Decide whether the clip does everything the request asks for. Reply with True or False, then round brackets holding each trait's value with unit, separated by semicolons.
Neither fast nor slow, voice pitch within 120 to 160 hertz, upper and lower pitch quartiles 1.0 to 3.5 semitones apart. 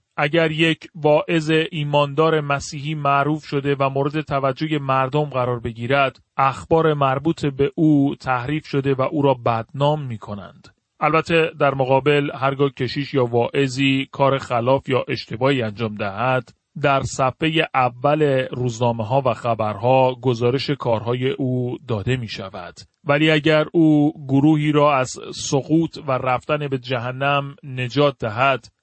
True (135 wpm; 140 Hz; 2.8 semitones)